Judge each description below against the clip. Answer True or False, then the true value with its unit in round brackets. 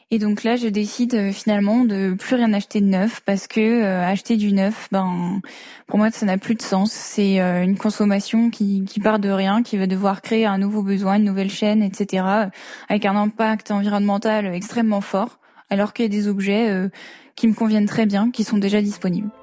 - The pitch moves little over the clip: True (2.0 semitones)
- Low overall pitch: False (205 Hz)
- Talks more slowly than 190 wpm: False (210 wpm)